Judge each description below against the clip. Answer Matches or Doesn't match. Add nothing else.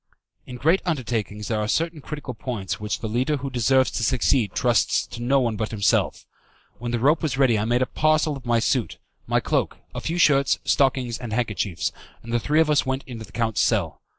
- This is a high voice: Doesn't match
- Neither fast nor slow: Doesn't match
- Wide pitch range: Doesn't match